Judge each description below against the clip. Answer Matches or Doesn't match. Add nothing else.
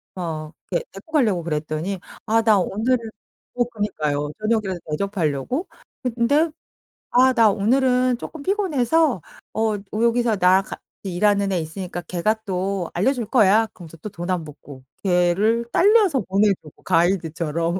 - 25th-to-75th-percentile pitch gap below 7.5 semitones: Matches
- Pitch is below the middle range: Doesn't match